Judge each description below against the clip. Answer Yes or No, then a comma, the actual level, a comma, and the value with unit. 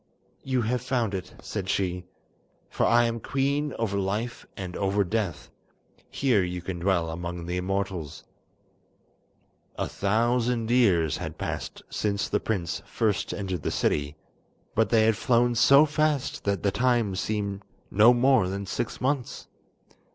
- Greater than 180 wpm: No, average, 145 wpm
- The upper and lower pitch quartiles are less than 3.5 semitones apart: No, average, 4.5 semitones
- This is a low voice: Yes, low, 105 Hz